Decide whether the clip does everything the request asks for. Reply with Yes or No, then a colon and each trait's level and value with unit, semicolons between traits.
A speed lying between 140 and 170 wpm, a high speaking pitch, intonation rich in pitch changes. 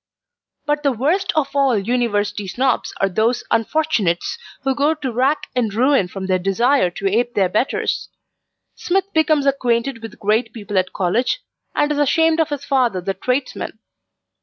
Yes: average, 160 wpm; high, 245 Hz; wide, 5.8 semitones